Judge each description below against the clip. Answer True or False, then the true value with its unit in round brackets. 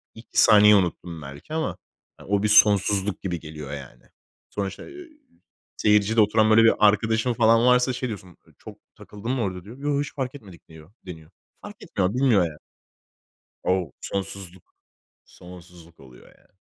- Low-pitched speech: True (100 Hz)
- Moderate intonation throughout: True (4.4 semitones)